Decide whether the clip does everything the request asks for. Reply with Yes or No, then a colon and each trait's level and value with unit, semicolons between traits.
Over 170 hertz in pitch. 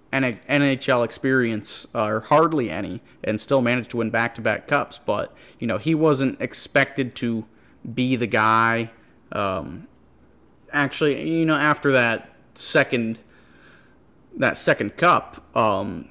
No: low, 125 Hz